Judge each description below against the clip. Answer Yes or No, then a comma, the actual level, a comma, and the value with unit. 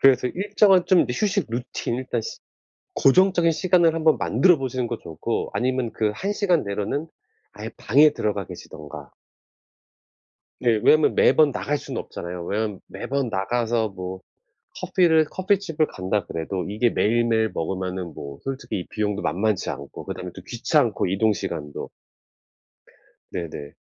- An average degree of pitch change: No, wide, 8.0 semitones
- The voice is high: No, low, 120 Hz